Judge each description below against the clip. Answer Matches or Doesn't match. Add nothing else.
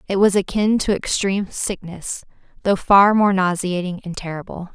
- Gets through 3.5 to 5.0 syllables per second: Matches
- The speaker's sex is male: Doesn't match